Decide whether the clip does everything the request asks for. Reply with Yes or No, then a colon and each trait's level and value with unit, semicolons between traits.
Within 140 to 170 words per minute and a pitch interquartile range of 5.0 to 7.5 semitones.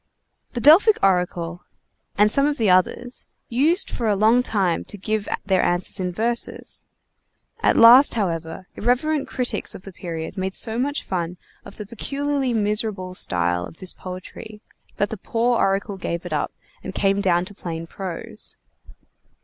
No: average, 160 wpm; average, 4.6 semitones